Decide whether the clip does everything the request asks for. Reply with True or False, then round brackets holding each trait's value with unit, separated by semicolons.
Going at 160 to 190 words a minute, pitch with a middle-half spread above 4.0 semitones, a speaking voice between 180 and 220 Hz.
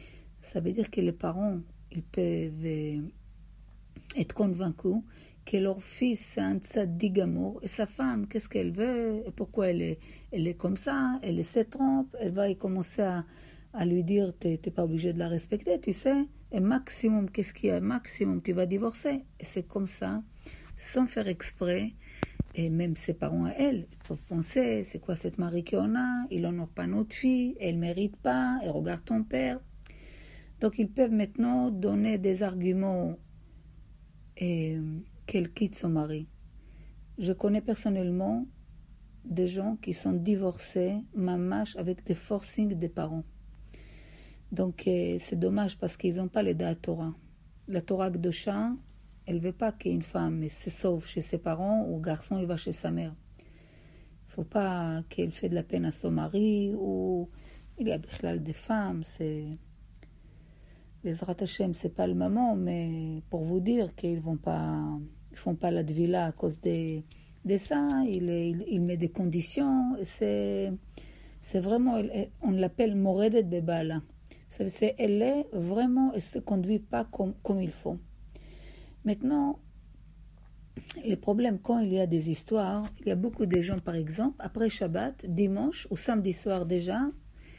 True (170 wpm; 4.7 semitones; 185 Hz)